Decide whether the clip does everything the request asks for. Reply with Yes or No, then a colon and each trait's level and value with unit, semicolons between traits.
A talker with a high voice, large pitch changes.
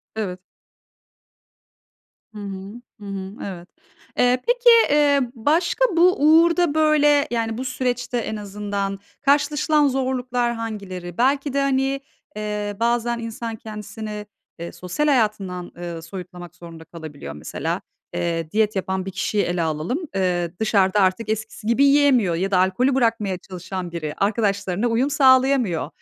Yes: high, 215 Hz; wide, 5.9 semitones